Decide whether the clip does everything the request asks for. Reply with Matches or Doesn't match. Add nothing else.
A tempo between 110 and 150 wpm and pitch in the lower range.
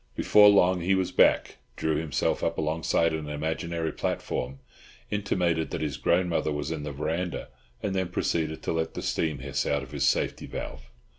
Doesn't match